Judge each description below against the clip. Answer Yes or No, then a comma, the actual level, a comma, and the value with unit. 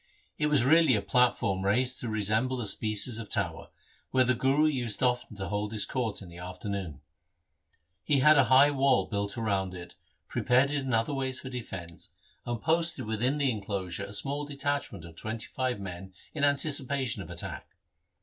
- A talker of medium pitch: No, low, 120 Hz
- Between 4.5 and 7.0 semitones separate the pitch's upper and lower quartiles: Yes, average, 5.0 semitones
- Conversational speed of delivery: Yes, average, 180 wpm